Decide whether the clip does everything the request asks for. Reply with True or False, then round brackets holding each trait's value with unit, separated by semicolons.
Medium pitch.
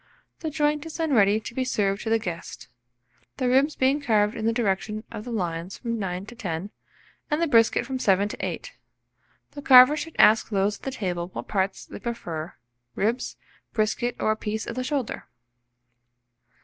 False (225 Hz)